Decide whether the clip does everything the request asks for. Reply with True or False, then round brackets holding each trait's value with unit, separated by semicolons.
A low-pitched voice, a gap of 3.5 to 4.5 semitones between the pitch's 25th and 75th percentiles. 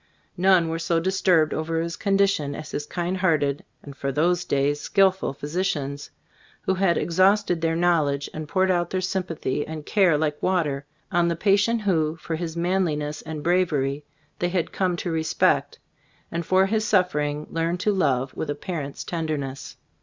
False (165 Hz; 3.8 semitones)